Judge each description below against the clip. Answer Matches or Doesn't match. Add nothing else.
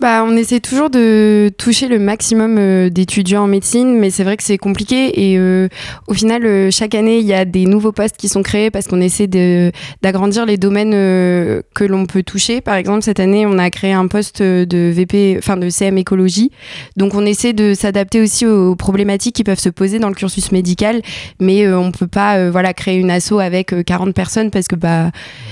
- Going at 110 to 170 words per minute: Doesn't match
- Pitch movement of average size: Doesn't match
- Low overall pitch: Doesn't match